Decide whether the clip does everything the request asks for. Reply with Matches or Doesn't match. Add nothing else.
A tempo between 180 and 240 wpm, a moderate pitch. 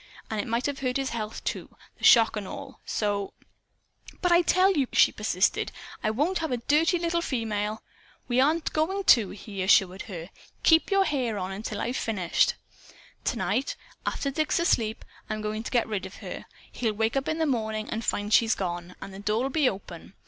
Doesn't match